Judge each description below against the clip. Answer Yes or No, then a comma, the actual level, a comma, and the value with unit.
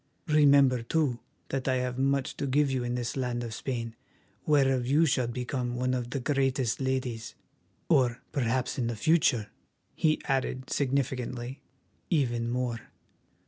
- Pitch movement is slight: Yes, narrow, 2.1 semitones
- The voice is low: Yes, low, 130 Hz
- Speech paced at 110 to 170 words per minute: Yes, average, 145 wpm